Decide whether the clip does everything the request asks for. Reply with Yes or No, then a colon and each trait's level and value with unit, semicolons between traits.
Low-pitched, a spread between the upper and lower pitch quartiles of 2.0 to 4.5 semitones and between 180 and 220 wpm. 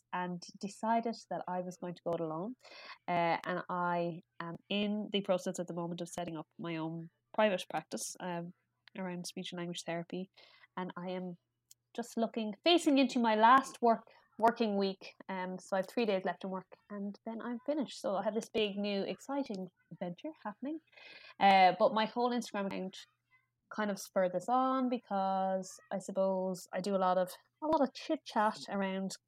No: high, 195 Hz; average, 4.0 semitones; average, 190 wpm